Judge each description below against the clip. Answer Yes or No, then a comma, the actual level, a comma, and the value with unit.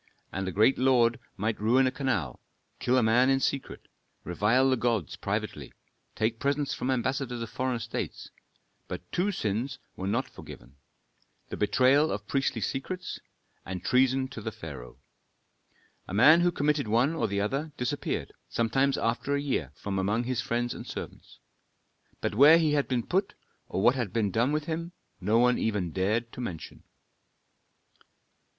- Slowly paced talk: No, average, 160 wpm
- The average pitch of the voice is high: No, low, 125 Hz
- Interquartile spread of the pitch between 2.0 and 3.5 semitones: No, average, 4.2 semitones